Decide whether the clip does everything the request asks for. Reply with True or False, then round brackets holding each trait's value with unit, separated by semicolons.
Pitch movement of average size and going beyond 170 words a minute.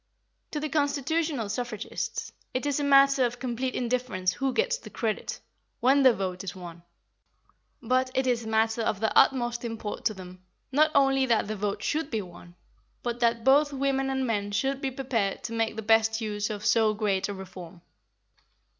True (4.3 semitones; 185 wpm)